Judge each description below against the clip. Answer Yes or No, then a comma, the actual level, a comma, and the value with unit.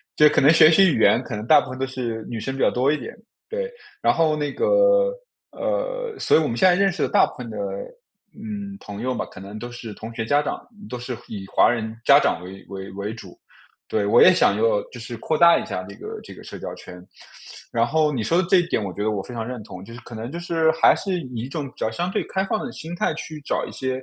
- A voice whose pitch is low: Yes, low, 130 Hz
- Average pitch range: No, wide, 7.3 semitones